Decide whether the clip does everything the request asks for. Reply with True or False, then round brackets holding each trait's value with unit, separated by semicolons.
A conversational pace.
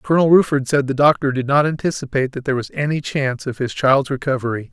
False (215 wpm)